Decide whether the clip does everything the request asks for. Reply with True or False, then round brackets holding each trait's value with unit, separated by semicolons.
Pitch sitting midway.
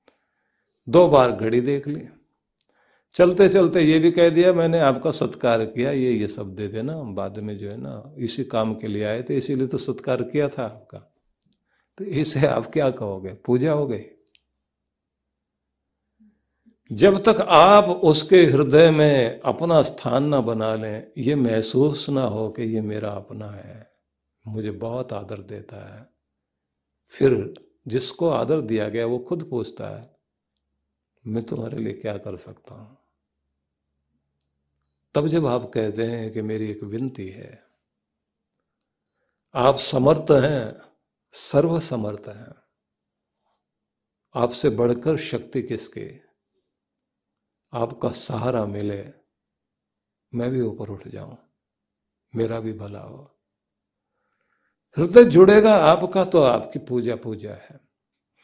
False (115 Hz)